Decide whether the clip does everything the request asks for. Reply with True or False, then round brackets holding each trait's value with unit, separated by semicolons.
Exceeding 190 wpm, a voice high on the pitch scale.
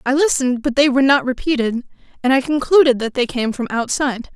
True (205 wpm; 260 Hz)